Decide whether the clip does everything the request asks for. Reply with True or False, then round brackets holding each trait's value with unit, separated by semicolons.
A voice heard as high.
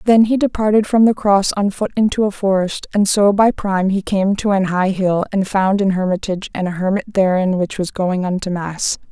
True (195 Hz)